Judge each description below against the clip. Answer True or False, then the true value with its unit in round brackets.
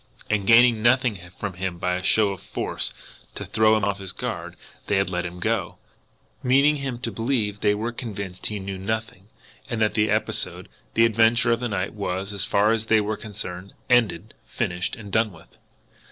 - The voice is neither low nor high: False (105 Hz)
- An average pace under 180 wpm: False (195 wpm)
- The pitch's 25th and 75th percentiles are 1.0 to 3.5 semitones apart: True (3.0 semitones)